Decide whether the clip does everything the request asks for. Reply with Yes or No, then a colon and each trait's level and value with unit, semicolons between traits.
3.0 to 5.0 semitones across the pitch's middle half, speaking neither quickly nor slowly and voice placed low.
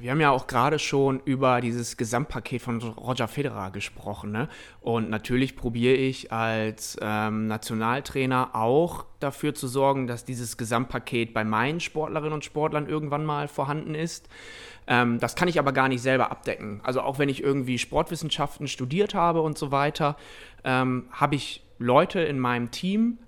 Yes: average, 4.0 semitones; average, 165 wpm; low, 130 Hz